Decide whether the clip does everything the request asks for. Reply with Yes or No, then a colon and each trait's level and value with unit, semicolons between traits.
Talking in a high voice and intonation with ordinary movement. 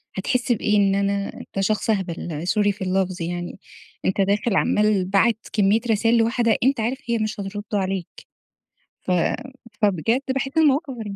Yes: high, 205 Hz; average, 3.0 semitones